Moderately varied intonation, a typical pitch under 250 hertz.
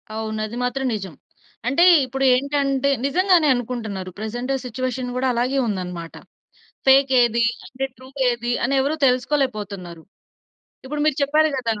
No: average, 3.8 semitones; very high, 255 Hz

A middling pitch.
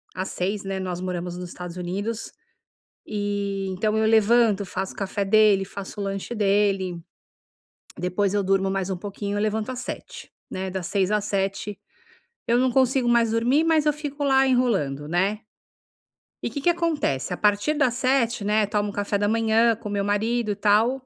No: high, 205 Hz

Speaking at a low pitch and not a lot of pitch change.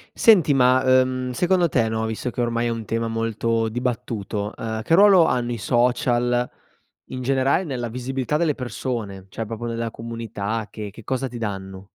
Yes: low, 120 Hz; narrow, 2.3 semitones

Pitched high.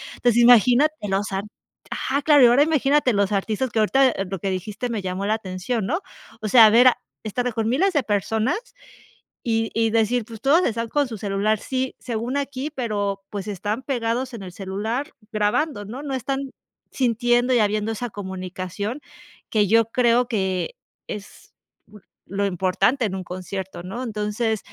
Yes: high, 225 Hz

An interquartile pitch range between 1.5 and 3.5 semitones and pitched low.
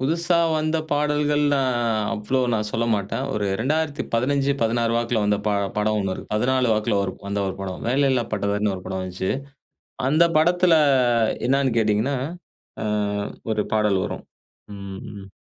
No: average, 5.3 semitones; low, 115 Hz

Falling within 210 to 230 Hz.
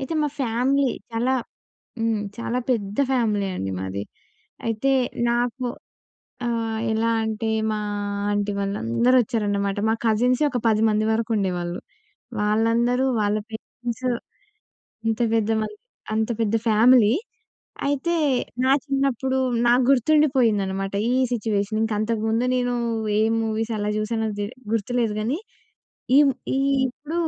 Yes: high, 225 Hz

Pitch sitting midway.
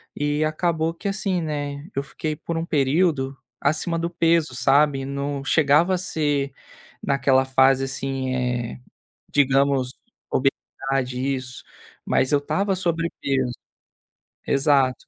Yes: medium, 145 Hz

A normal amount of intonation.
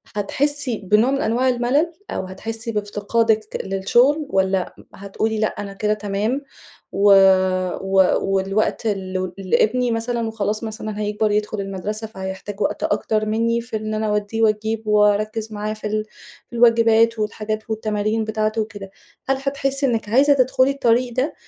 No: narrow, 2.0 semitones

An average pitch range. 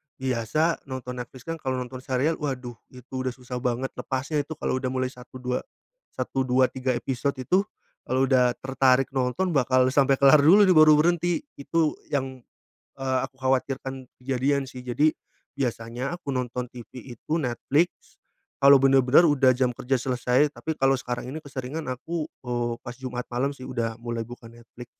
No: narrow, 2.0 semitones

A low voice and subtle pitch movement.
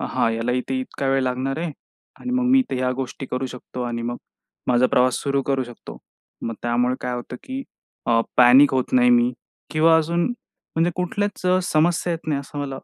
No: low, 130 Hz; average, 4.6 semitones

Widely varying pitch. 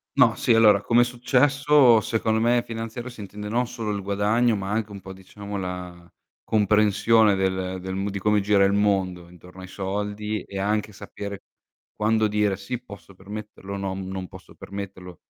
No: narrow, 2.5 semitones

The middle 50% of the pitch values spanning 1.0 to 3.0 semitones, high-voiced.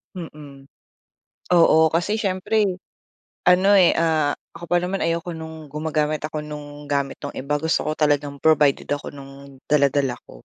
No: narrow, 2.6 semitones; medium, 155 Hz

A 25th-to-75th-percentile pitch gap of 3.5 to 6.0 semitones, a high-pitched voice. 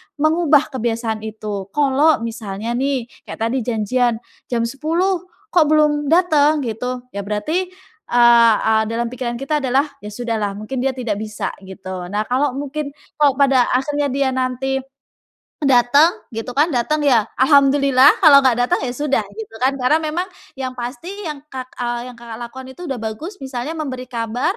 Yes: average, 3.8 semitones; very high, 255 Hz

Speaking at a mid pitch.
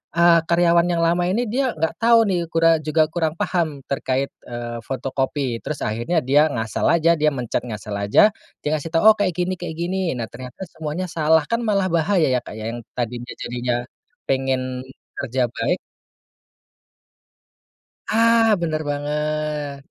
Yes: medium, 155 Hz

